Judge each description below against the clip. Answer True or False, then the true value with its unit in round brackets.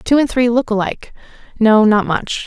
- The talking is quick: False (170 wpm)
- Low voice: False (225 Hz)